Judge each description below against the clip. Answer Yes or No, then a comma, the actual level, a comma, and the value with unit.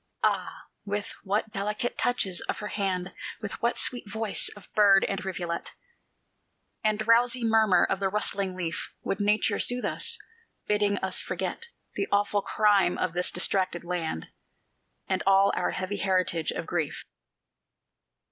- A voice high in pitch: Yes, high, 200 Hz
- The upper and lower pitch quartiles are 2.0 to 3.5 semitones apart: Yes, narrow, 2.4 semitones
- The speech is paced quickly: No, average, 145 wpm